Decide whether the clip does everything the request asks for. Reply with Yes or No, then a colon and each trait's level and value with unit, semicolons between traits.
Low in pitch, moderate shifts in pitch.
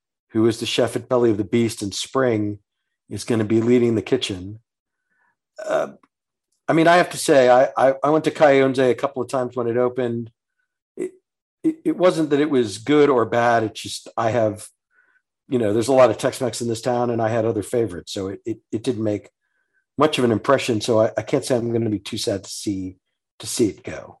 Yes: low, 125 Hz; average, 4.2 semitones